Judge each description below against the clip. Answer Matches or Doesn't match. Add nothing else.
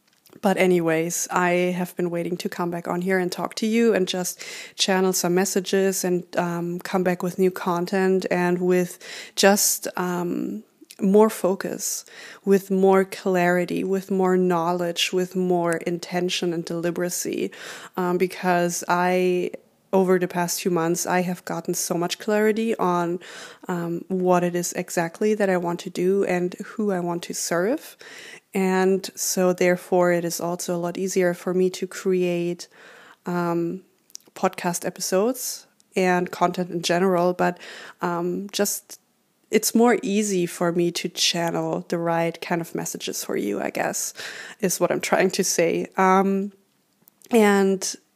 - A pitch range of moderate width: Doesn't match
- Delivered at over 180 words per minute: Doesn't match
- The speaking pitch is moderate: Matches